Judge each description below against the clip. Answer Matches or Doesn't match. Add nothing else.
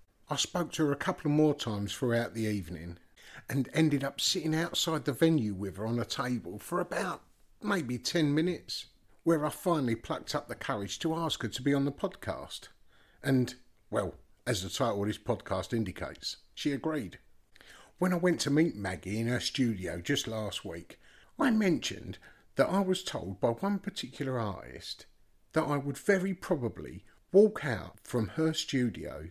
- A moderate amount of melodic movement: Doesn't match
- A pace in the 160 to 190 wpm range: Matches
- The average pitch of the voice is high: Doesn't match